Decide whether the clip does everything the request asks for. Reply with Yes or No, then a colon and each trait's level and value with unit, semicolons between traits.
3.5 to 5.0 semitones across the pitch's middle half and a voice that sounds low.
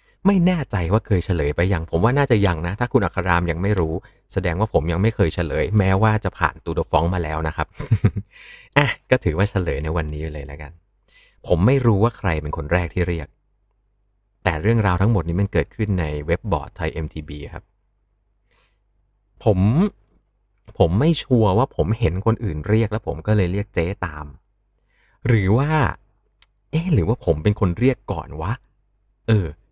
Yes: average, 4.7 semitones; low, 100 Hz